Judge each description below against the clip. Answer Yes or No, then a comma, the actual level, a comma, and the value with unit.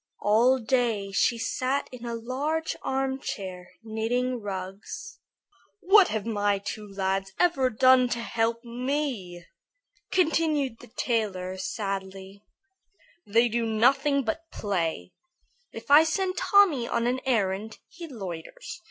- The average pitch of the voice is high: Yes, high, 235 Hz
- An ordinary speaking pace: No, slow, 120 wpm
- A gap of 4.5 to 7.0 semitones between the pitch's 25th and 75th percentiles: Yes, average, 5.1 semitones